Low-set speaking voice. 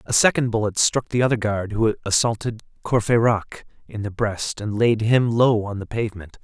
Yes: low, 110 Hz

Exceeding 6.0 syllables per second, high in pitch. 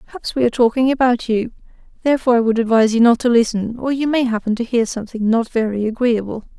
Yes: 6.9 syllables/s; high, 235 Hz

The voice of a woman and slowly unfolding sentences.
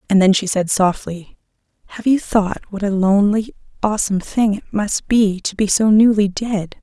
No: female; average, 185 wpm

